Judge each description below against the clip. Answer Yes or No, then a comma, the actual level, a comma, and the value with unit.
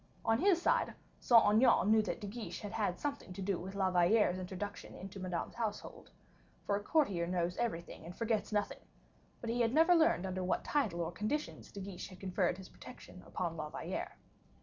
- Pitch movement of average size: Yes, average, 4.0 semitones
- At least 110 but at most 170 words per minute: No, average, 195 wpm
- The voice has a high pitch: Yes, high, 200 Hz